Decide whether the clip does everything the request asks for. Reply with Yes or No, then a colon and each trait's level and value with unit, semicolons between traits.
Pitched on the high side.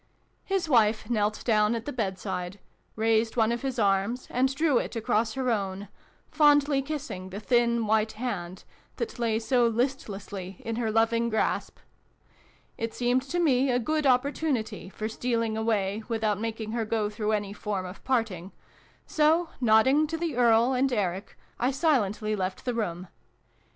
Yes: high, 225 Hz